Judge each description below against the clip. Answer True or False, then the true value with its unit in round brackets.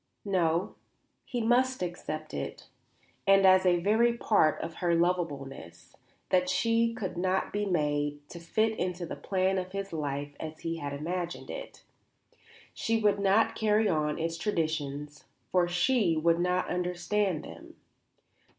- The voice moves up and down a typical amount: True (4.1 semitones)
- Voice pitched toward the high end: False (180 Hz)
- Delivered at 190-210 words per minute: False (145 wpm)